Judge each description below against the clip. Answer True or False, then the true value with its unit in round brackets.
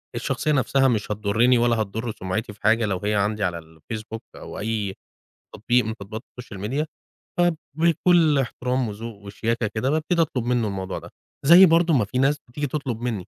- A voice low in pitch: True (115 Hz)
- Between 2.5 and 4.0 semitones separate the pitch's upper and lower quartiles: False (4.6 semitones)